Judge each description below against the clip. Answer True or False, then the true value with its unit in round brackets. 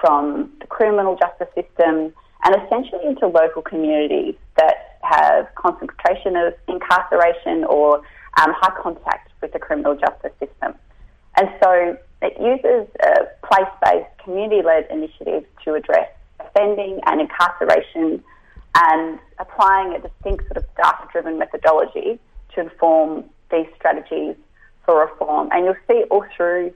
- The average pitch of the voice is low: False (185 Hz)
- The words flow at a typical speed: False (125 wpm)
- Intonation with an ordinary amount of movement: False (5.9 semitones)